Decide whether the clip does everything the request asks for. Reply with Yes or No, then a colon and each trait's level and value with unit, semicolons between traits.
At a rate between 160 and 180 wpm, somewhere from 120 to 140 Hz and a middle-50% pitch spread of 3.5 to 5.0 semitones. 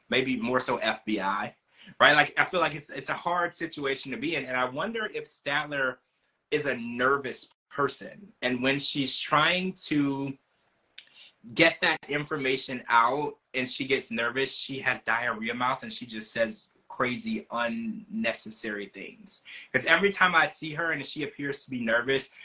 Yes: average, 165 wpm; low, 135 Hz; average, 4.7 semitones